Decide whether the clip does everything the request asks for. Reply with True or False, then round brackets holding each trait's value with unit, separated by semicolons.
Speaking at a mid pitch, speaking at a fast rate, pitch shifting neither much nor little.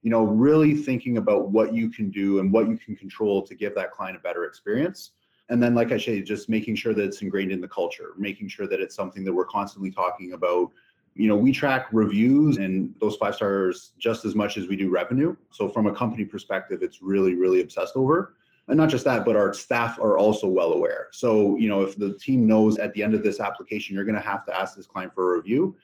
False (110 Hz; 245 wpm; 3.8 semitones)